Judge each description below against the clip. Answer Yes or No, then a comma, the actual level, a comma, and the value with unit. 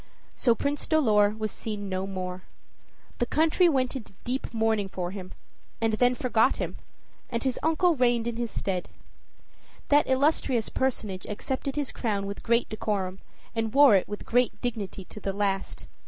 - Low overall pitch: No, high, 225 Hz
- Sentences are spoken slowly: No, average, 165 wpm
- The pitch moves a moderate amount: Yes, average, 4.5 semitones